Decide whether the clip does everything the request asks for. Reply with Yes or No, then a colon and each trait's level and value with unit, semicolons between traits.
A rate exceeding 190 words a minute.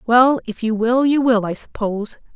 Yes: fast, 205 wpm